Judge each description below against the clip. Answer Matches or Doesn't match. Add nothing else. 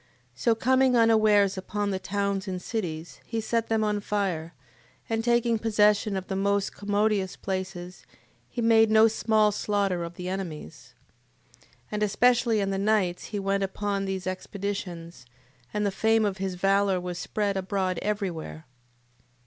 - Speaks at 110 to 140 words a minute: Doesn't match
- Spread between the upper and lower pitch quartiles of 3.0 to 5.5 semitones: Doesn't match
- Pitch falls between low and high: Doesn't match